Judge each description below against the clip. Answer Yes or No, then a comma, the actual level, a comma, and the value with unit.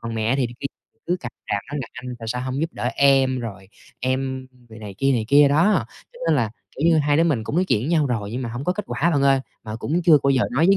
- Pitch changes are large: No, average, 4.2 semitones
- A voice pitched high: No, low, 135 Hz